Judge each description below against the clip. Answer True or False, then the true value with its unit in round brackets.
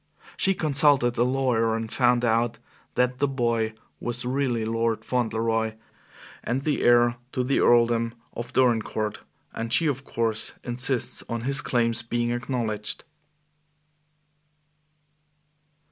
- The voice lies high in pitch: False (120 Hz)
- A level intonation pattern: True (1.9 semitones)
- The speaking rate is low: True (120 wpm)